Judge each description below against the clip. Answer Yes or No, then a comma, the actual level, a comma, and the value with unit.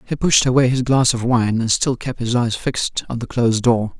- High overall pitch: No, low, 120 Hz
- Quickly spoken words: Yes, fast, 255 wpm